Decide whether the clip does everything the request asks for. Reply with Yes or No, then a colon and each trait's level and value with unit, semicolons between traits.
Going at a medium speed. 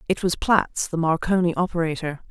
Yes: average, 155 wpm